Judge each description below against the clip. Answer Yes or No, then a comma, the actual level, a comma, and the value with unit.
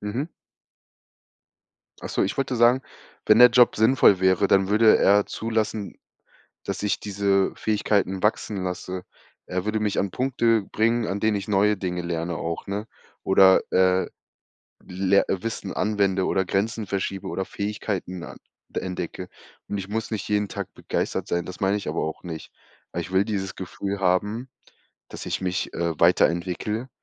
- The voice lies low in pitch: Yes, low, 100 Hz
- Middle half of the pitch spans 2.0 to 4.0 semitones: Yes, narrow, 2.5 semitones